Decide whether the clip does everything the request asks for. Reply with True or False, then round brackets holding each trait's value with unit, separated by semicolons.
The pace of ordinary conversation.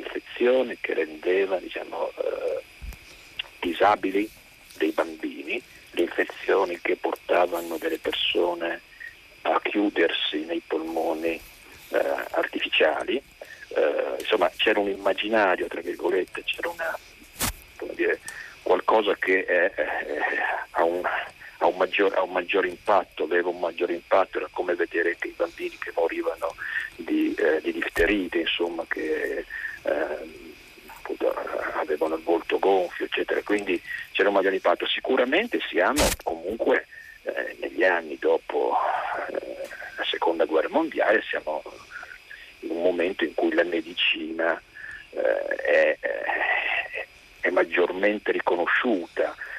False (105 wpm)